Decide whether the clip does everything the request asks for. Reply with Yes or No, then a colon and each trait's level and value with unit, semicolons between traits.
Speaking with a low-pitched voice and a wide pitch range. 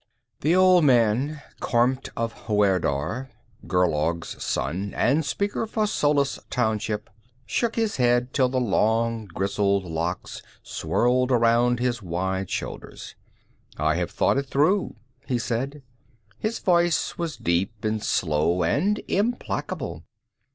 Yes: low, 120 Hz; wide, 6.5 semitones